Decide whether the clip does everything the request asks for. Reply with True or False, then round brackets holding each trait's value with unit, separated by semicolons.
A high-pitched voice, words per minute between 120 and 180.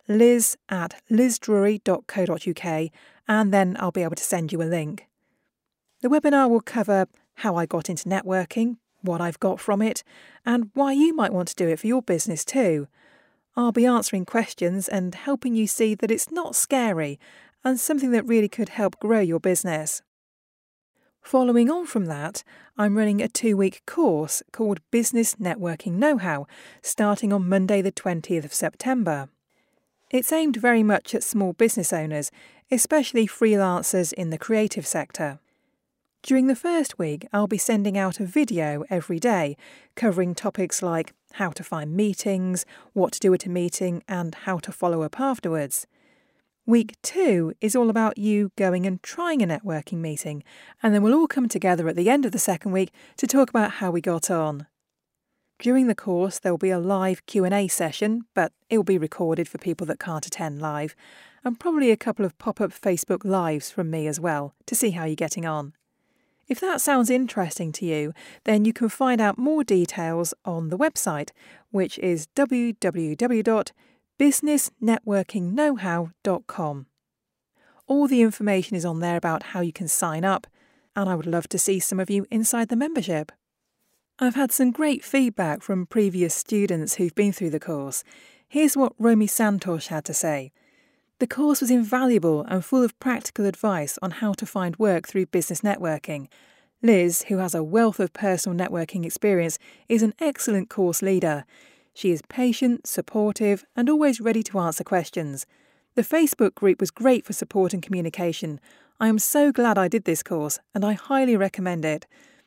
True (200 Hz; 170 wpm)